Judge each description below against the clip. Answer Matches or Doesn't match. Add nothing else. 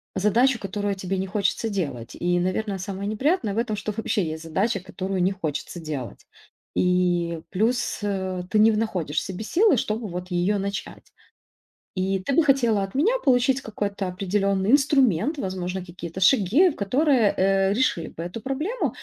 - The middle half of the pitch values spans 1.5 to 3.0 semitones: Doesn't match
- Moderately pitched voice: Doesn't match